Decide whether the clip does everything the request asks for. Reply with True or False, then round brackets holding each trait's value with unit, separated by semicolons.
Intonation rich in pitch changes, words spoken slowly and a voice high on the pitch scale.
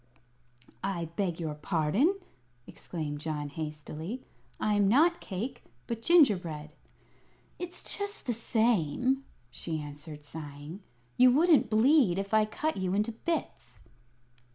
True (8.4 semitones; 120 wpm; 195 Hz)